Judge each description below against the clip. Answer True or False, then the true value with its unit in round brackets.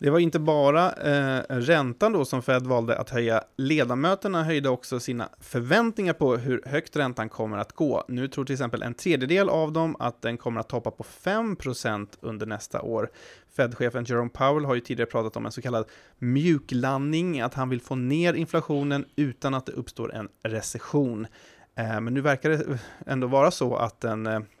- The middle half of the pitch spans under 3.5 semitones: False (4.1 semitones)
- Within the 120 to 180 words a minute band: False (190 wpm)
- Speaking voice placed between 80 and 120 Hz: False (130 Hz)